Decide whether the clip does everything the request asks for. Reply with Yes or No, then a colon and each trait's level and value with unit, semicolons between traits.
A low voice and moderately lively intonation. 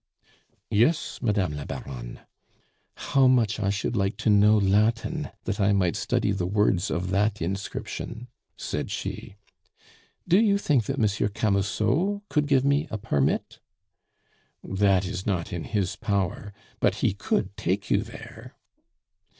Yes: low, 105 Hz; average, 4.0 semitones